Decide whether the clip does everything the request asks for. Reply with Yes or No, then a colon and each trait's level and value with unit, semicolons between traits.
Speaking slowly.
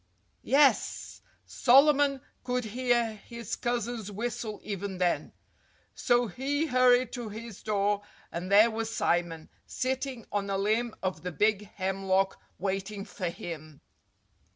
Yes: slow, 125 wpm